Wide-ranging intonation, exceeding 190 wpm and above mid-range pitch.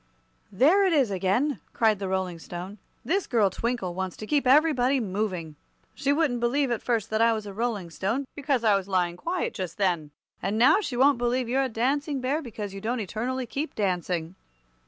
Yes: wide, 5.7 semitones; average, 200 wpm; high, 230 Hz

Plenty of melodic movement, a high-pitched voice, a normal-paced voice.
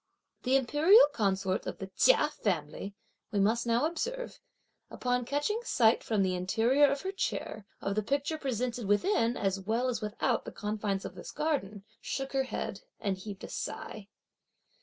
Yes: wide, 5.8 semitones; high, 235 Hz; average, 165 wpm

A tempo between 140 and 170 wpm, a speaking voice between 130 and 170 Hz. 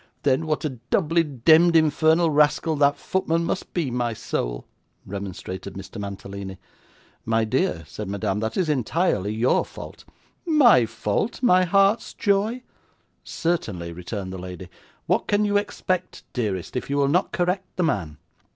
Yes: average, 150 wpm; medium, 140 Hz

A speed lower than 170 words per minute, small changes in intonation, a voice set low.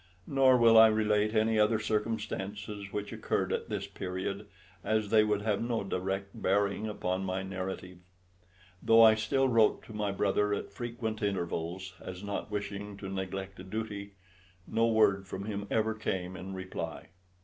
Yes: average, 160 wpm; narrow, 2.2 semitones; low, 105 Hz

